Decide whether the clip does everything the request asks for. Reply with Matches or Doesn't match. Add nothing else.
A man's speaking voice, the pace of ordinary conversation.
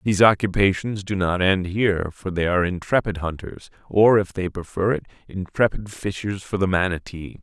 Matches